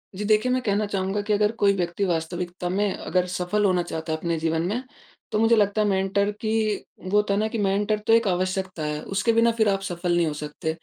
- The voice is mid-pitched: No, high, 195 Hz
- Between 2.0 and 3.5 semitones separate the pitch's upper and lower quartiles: Yes, average, 3.0 semitones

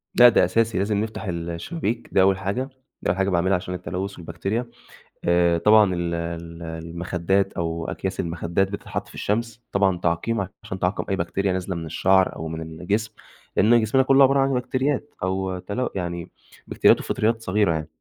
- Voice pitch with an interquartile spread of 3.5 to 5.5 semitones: Yes, average, 4.2 semitones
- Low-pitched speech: Yes, very low, 95 Hz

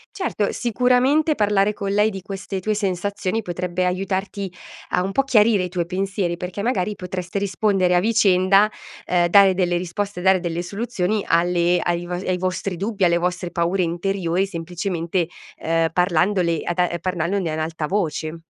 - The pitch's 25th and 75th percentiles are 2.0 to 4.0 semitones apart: Yes, narrow, 2.4 semitones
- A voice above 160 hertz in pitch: Yes, medium, 185 Hz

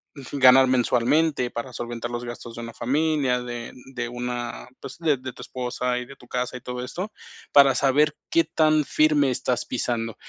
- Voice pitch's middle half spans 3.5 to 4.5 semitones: No, average, 2.7 semitones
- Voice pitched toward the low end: Yes, low, 125 Hz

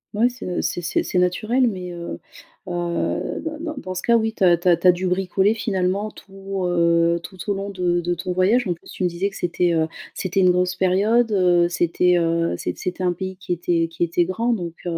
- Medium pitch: Yes, medium, 180 Hz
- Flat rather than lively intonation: Yes, narrow, 2.2 semitones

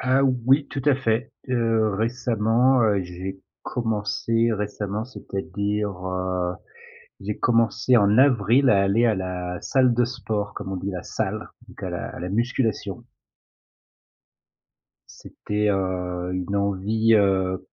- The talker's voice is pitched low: Yes, low, 105 Hz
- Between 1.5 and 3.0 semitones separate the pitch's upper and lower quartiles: No, average, 3.5 semitones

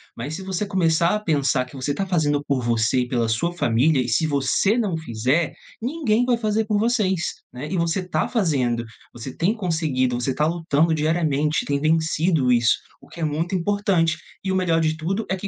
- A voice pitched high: No, medium, 160 Hz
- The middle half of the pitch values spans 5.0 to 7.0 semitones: Yes, wide, 5.4 semitones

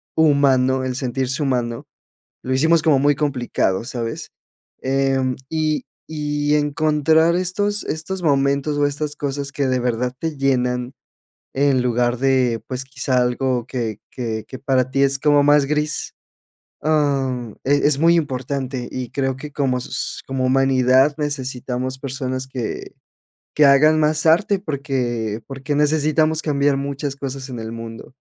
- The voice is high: No, low, 135 Hz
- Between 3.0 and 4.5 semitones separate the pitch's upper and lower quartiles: No, narrow, 2.5 semitones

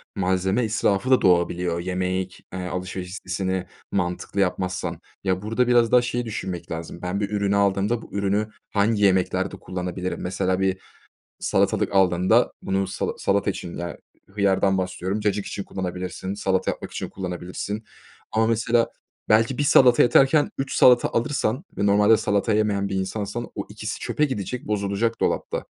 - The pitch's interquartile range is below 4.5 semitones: Yes, average, 2.8 semitones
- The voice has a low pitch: Yes, low, 100 Hz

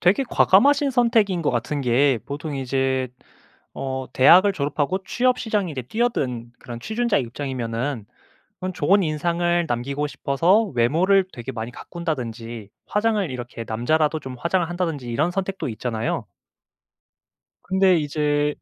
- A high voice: No, medium, 150 Hz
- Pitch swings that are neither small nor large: No, wide, 6.8 semitones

